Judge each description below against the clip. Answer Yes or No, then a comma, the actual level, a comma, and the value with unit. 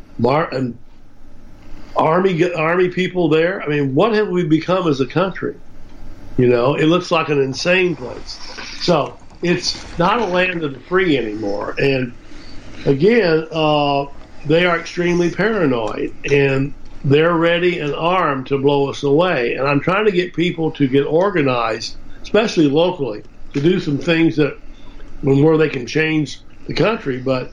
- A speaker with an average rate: Yes, average, 155 wpm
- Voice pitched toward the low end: No, medium, 150 Hz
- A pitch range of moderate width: Yes, average, 4.6 semitones